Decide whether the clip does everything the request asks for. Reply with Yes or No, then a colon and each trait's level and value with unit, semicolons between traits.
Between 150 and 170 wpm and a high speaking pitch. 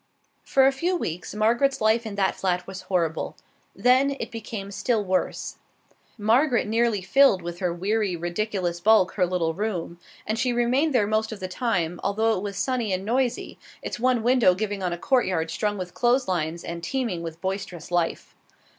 No: average, 180 wpm; high, 205 Hz